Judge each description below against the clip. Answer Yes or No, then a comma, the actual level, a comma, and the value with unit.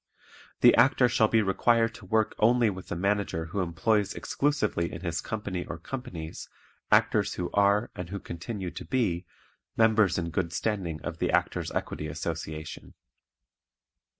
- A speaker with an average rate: Yes, average, 150 wpm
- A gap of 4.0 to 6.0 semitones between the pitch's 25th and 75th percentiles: Yes, average, 4.7 semitones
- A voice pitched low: Yes, very low, 95 Hz